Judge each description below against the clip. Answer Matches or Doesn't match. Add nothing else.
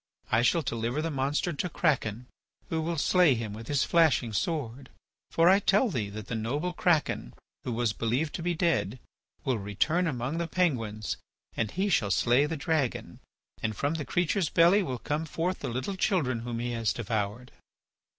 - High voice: Doesn't match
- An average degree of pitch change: Doesn't match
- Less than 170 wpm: Doesn't match